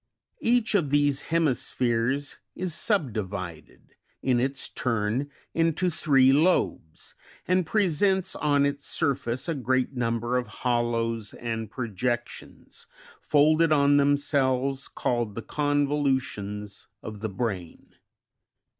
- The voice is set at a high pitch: No, low, 130 Hz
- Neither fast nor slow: No, slow, 110 wpm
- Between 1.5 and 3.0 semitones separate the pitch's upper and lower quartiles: No, average, 4.2 semitones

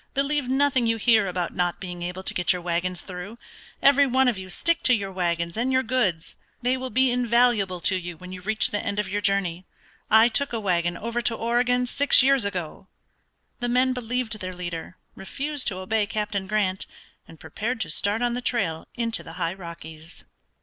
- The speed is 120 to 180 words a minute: No, average, 200 wpm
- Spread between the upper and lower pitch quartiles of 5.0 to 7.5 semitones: Yes, wide, 5.4 semitones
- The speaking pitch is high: Yes, high, 210 Hz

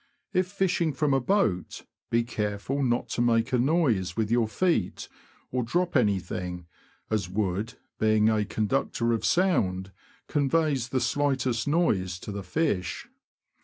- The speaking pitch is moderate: No, low, 120 Hz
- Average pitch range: No, wide, 5.8 semitones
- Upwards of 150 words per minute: No, average, 140 wpm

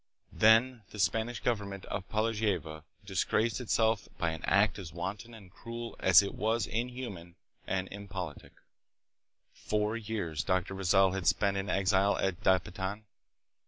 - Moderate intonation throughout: Yes, average, 3.0 semitones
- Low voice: Yes, low, 100 Hz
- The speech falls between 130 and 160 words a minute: Yes, average, 145 wpm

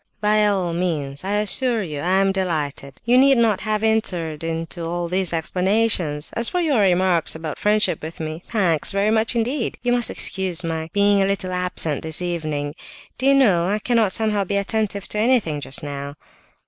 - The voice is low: No, high, 190 Hz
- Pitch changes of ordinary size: Yes, average, 4.6 semitones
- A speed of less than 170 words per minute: No, average, 180 wpm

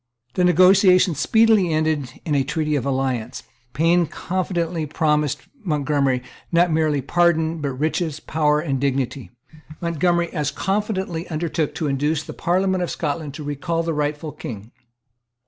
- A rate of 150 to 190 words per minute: No, average, 140 wpm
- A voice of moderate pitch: Yes, medium, 155 Hz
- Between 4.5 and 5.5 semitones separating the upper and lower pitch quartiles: No, average, 3.2 semitones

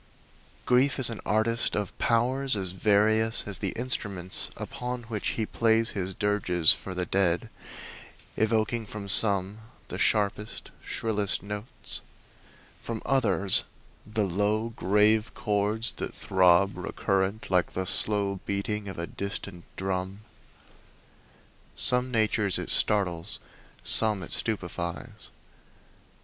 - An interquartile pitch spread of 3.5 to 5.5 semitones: No, narrow, 2.6 semitones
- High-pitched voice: No, low, 105 Hz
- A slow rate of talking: Yes, slow, 115 wpm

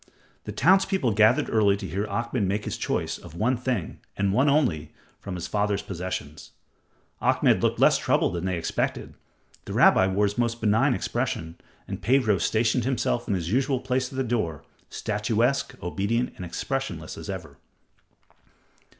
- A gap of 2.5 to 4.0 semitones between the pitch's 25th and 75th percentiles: No, average, 4.7 semitones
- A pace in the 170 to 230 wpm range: No, average, 160 wpm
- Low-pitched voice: Yes, low, 110 Hz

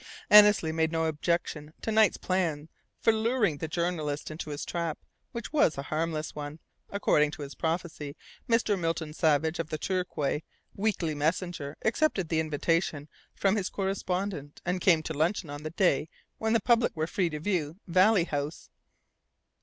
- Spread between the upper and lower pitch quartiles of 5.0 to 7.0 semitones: No, average, 3.8 semitones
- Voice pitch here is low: No, medium, 165 Hz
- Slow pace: No, average, 160 wpm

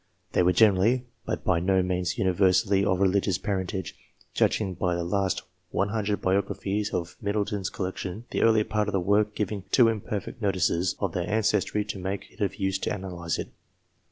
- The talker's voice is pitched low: Yes, low, 100 Hz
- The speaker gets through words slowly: No, average, 180 wpm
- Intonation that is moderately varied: No, narrow, 2.1 semitones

